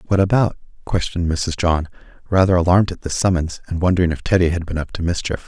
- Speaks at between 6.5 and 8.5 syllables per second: Yes, 6.6 syllables/s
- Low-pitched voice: Yes, very low, 85 Hz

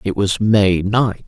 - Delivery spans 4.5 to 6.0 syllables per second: No, 3.5 syllables/s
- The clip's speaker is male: No, female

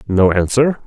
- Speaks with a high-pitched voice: No, low, 110 Hz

